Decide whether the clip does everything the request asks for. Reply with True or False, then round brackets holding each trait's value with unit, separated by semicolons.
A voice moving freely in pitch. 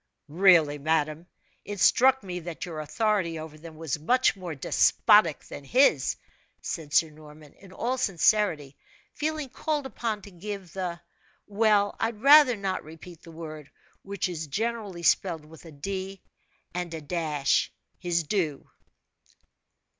False (4.9 semitones)